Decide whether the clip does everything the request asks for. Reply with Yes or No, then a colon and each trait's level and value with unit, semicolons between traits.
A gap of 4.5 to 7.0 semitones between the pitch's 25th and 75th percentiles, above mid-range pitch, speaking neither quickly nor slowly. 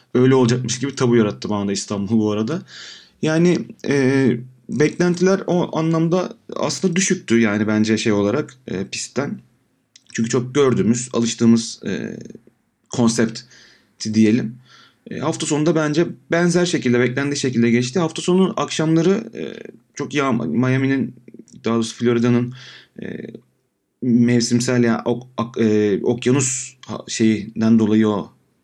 No: average, 5.0 semitones; low, 125 Hz; average, 120 wpm